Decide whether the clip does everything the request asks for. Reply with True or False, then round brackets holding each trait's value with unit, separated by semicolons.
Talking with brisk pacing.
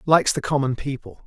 False (190 wpm)